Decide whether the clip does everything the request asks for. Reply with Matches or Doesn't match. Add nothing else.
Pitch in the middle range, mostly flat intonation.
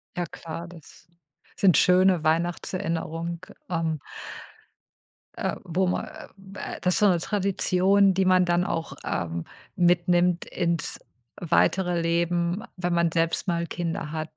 Matches